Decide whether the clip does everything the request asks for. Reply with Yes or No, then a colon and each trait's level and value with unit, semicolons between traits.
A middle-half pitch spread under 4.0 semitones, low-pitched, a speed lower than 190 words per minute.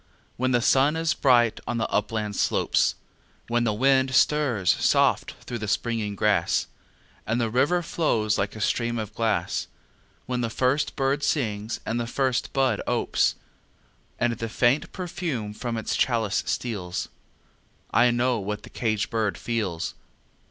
Yes: average, 3.3 semitones; low, 120 Hz; average, 150 wpm